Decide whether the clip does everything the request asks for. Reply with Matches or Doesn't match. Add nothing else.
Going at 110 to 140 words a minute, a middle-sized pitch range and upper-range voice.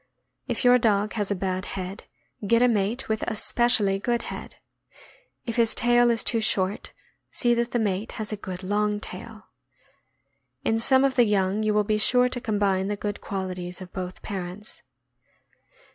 Doesn't match